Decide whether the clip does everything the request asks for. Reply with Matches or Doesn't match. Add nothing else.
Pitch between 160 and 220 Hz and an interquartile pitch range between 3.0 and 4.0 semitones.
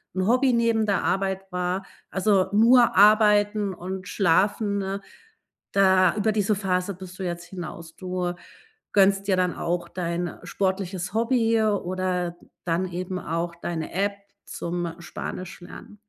Doesn't match